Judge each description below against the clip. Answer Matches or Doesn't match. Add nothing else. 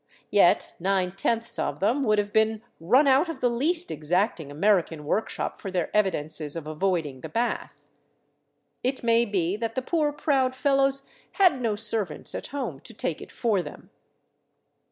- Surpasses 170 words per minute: Doesn't match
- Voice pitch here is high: Matches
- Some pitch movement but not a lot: Doesn't match